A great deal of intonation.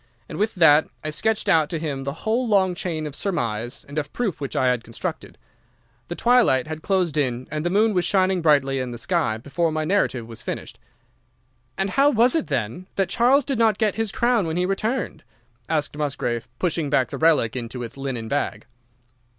Yes: wide, 6.6 semitones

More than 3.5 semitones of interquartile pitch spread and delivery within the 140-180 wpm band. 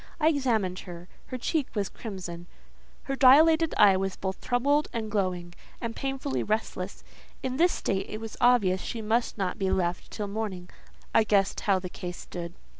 Yes: average, 5.3 semitones; average, 175 wpm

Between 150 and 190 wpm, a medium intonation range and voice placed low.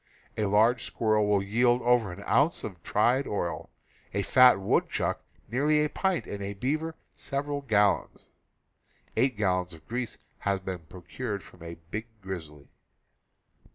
Yes: average, 155 wpm; average, 4.9 semitones; low, 105 Hz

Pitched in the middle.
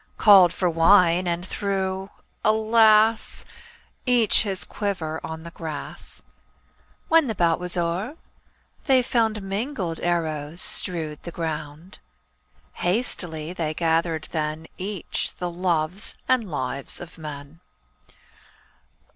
Yes: medium, 175 Hz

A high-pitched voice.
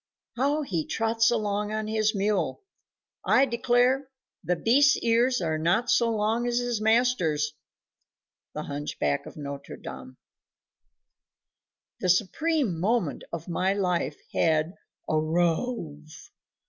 Yes: high, 210 Hz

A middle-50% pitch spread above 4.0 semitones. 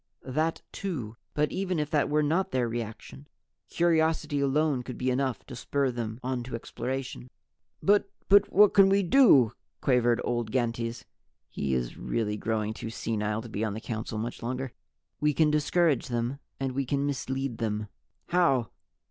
Yes: average, 4.6 semitones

